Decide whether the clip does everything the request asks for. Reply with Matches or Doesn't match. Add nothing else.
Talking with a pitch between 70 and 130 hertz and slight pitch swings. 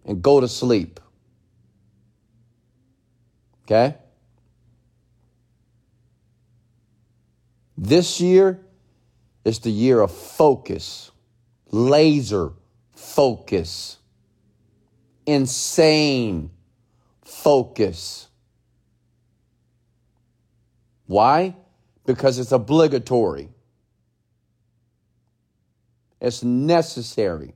Matches